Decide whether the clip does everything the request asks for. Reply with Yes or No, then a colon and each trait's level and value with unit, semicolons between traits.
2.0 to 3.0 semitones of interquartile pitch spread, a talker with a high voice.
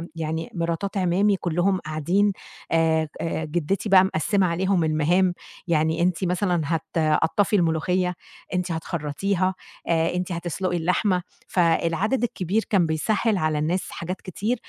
No: average, 2.7 semitones; medium, 175 Hz